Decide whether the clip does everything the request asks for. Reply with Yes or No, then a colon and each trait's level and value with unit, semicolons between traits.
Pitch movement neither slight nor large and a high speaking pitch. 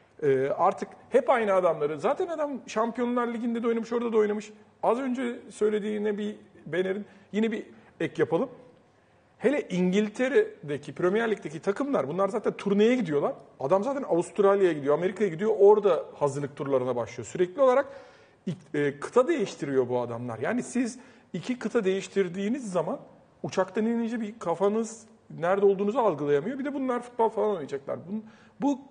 Yes: average, 4.9 semitones; high, 210 Hz